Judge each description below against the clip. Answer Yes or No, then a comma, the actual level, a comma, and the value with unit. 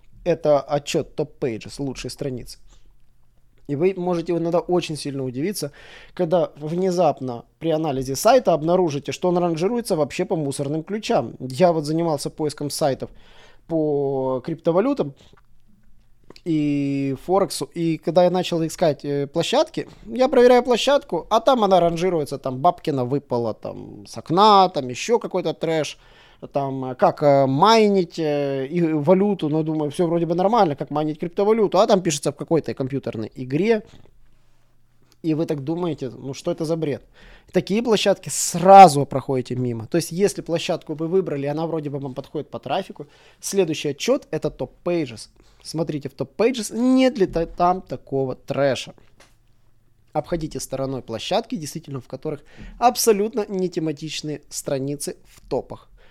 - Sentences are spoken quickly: No, average, 140 wpm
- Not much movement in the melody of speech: No, average, 4.8 semitones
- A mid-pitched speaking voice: Yes, medium, 155 Hz